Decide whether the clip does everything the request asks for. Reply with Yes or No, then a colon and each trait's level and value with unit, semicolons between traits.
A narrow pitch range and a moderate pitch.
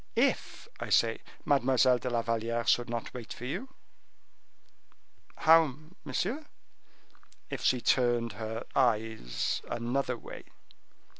No: narrow, 2.2 semitones; low, 120 Hz